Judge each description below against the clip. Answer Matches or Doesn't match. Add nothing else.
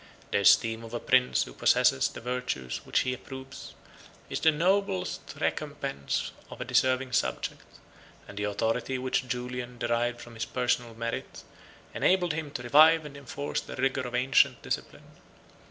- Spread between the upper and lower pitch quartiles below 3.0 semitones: Matches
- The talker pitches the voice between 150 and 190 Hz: Doesn't match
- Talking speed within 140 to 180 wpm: Matches